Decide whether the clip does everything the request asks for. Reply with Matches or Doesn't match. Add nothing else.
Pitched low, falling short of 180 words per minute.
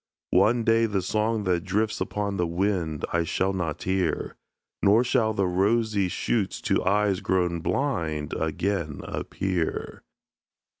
Matches